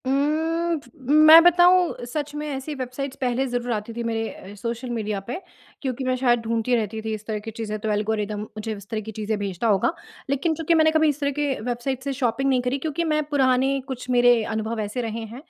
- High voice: Yes, high, 245 Hz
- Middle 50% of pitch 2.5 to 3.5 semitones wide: No, average, 4.2 semitones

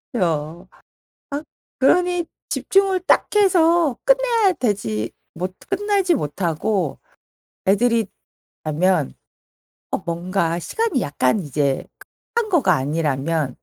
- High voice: Yes, high, 195 Hz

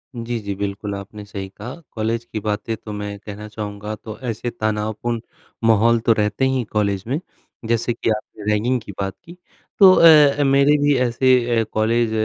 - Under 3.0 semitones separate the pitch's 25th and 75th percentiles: Yes, narrow, 2.4 semitones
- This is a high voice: No, low, 110 Hz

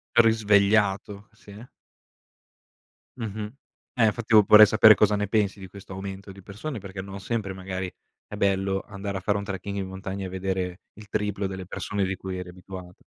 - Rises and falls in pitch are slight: Yes, narrow, 1.7 semitones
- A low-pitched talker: Yes, low, 100 Hz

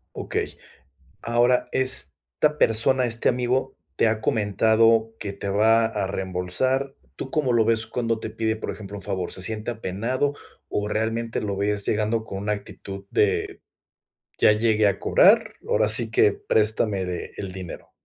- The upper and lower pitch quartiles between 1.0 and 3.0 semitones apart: Yes, narrow, 2.4 semitones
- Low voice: Yes, low, 110 Hz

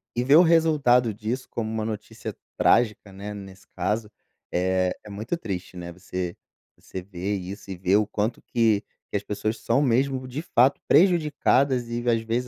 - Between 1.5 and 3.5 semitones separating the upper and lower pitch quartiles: No, average, 4.3 semitones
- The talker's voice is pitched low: Yes, low, 110 Hz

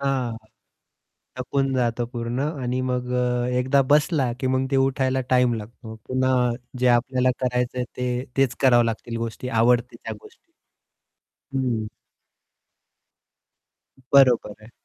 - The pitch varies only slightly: Yes, narrow, 1.5 semitones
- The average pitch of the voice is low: Yes, low, 125 Hz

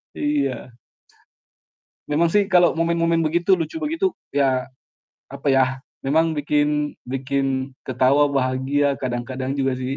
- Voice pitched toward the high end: No, medium, 140 Hz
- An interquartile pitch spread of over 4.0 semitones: No, average, 3.6 semitones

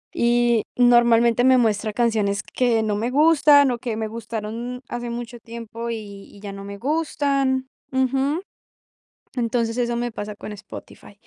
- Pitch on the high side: Yes, high, 235 Hz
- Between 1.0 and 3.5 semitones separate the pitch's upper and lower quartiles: Yes, narrow, 2.4 semitones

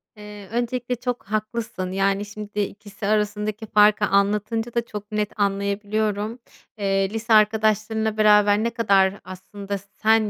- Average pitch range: No, narrow, 1.4 semitones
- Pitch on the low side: No, high, 210 Hz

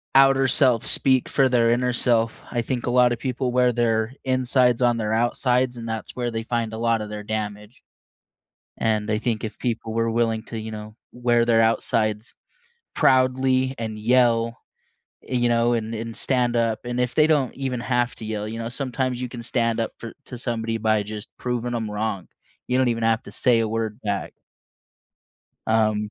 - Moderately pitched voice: No, low, 115 Hz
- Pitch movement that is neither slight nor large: No, narrow, 1.9 semitones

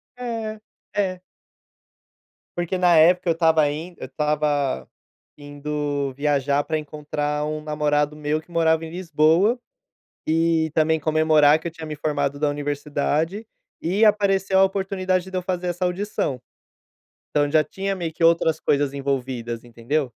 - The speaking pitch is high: No, medium, 155 Hz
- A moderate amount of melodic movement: Yes, average, 3.4 semitones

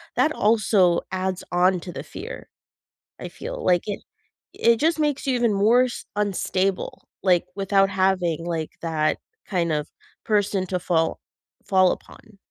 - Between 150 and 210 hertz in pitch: Yes, high, 190 Hz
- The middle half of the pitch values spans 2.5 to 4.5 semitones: Yes, average, 3.3 semitones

